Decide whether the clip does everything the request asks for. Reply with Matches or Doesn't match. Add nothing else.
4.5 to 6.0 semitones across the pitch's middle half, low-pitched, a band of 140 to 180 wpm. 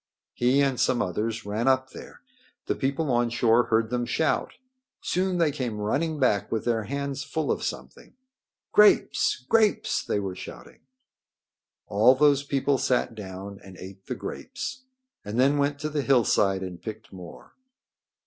Matches